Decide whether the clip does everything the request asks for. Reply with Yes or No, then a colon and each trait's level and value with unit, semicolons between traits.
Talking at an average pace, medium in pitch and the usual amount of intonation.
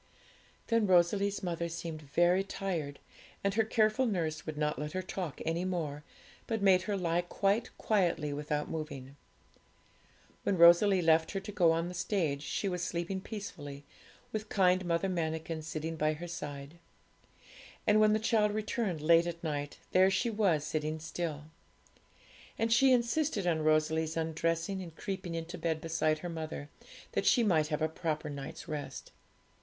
Yes: average, 160 wpm; medium, 170 Hz; average, 3.8 semitones